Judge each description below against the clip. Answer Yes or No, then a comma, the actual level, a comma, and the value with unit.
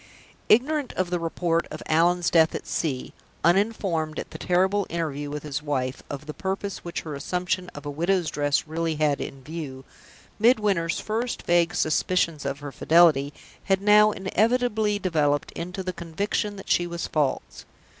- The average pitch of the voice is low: No, medium, 170 Hz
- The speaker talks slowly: No, average, 165 wpm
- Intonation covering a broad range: No, average, 4.3 semitones